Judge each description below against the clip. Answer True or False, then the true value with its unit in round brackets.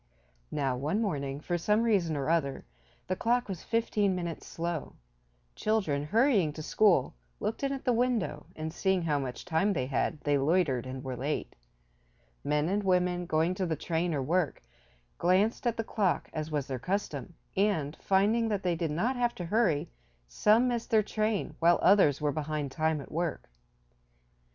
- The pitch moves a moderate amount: False (5.9 semitones)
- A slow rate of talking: False (175 wpm)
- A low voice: False (175 Hz)